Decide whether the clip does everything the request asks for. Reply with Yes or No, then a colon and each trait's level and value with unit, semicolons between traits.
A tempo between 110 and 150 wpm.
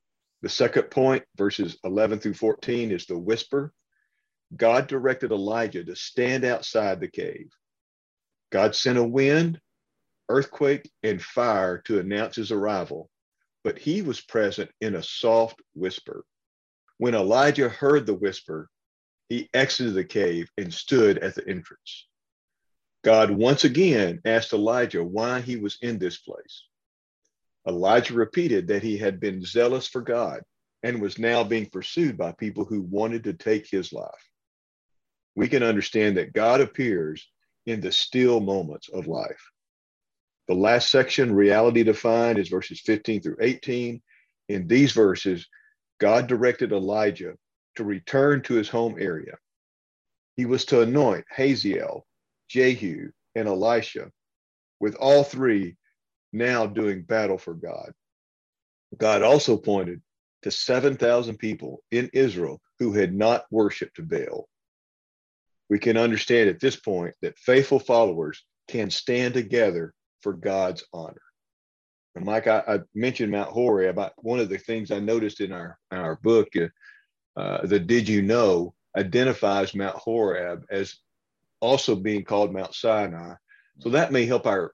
Yes: average, 140 wpm